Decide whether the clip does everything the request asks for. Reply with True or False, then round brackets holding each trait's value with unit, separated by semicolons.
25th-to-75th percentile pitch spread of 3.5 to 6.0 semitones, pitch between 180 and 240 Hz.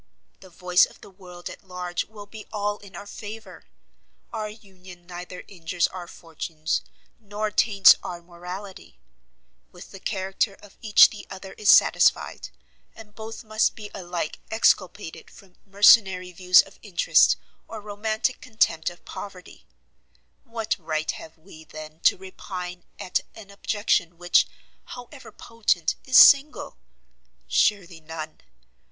False (3.1 semitones; 190 Hz)